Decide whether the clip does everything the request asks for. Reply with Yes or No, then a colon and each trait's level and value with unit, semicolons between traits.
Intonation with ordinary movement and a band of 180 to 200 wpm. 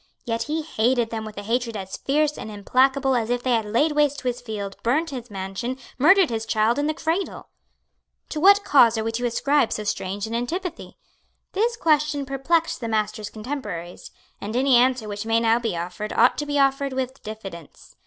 Yes: average, 4.9 semitones; average, 195 wpm